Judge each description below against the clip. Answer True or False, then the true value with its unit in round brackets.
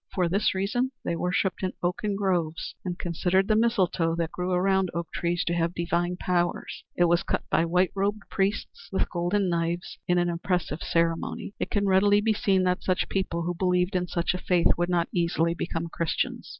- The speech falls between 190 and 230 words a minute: True (195 wpm)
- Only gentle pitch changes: True (2.0 semitones)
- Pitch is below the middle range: False (180 Hz)